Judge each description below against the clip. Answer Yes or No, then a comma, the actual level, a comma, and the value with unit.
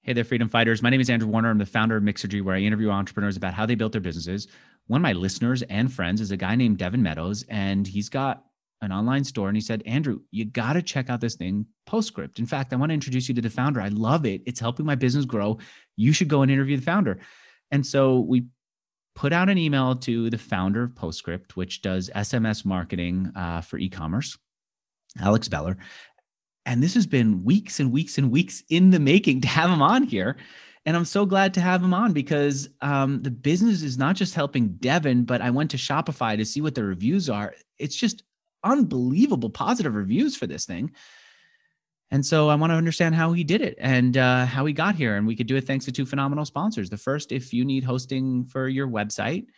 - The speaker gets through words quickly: Yes, fast, 230 wpm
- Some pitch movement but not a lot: No, wide, 5.7 semitones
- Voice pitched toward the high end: No, low, 130 Hz